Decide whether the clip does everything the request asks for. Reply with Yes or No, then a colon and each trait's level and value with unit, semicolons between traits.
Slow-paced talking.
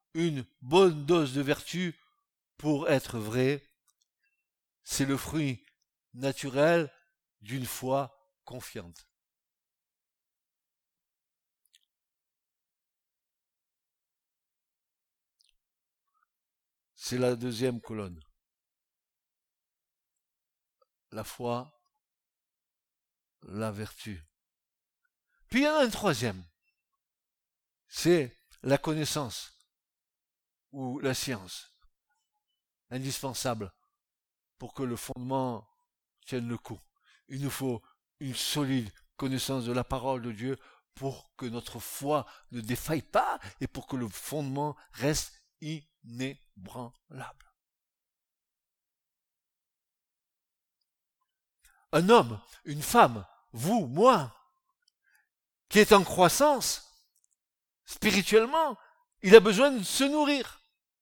Yes: slow, 85 wpm